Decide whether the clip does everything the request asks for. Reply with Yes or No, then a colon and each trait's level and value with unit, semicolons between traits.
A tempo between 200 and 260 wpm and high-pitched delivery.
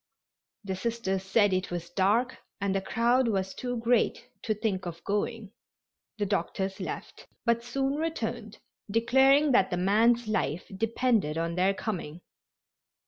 No: average, 140 wpm; high, 210 Hz